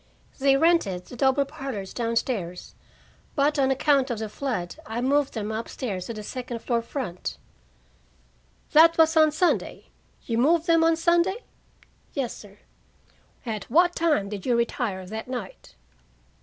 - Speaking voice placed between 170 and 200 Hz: No, very high, 255 Hz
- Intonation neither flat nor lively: No, wide, 5.8 semitones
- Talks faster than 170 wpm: No, average, 155 wpm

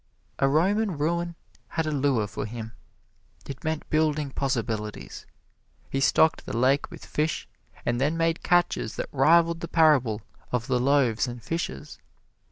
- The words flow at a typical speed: Yes, average, 150 wpm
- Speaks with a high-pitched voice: No, medium, 145 Hz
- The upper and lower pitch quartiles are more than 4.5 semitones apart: Yes, average, 4.9 semitones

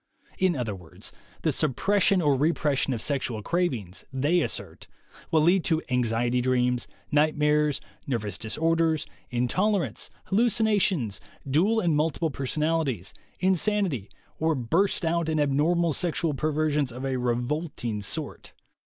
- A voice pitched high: No, medium, 150 Hz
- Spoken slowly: Yes, slow, 125 wpm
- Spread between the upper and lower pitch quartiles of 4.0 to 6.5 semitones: Yes, average, 5.2 semitones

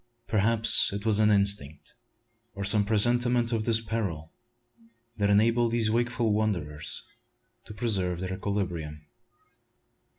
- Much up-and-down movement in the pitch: No, average, 3.3 semitones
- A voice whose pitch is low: Yes, low, 105 Hz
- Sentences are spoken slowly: Yes, slow, 120 wpm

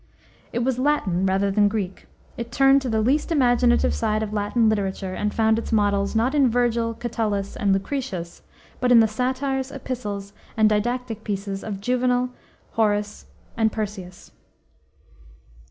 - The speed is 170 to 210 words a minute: No, average, 150 wpm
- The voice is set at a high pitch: Yes, high, 220 Hz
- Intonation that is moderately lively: Yes, average, 3.5 semitones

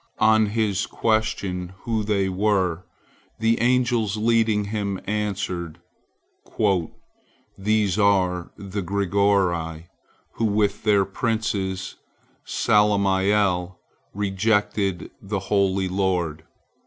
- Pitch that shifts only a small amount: Yes, narrow, 2.2 semitones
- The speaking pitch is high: No, low, 100 Hz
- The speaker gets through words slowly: Yes, slow, 85 wpm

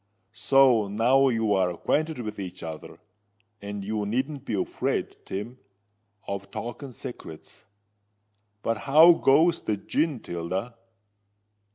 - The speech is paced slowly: Yes, slow, 110 wpm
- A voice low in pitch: Yes, low, 115 Hz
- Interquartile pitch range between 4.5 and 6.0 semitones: Yes, wide, 5.4 semitones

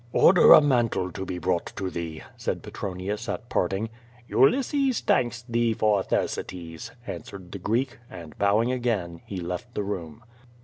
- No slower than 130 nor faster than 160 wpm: Yes, average, 150 wpm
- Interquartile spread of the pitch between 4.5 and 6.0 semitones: Yes, average, 4.8 semitones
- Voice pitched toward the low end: Yes, low, 100 Hz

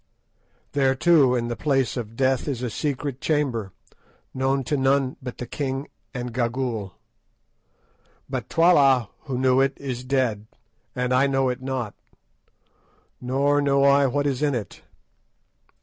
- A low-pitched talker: Yes, low, 130 Hz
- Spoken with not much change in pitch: Yes, narrow, 2.0 semitones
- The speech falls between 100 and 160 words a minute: Yes, average, 145 wpm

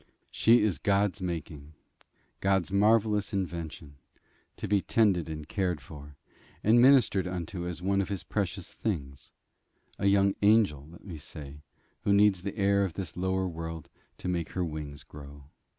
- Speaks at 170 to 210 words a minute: No, average, 155 wpm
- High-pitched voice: No, very low, 90 Hz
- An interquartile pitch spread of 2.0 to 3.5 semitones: No, average, 4.2 semitones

